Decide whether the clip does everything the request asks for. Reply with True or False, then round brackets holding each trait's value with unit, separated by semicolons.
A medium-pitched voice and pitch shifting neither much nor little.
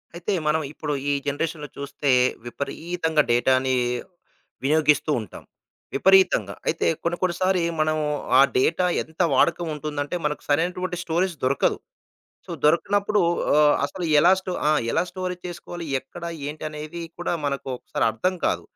True (160 Hz; 3.4 semitones)